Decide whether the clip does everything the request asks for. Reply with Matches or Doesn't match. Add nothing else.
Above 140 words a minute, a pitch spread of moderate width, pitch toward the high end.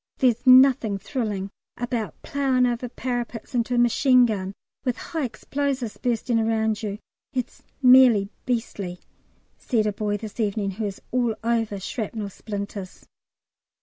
Doesn't match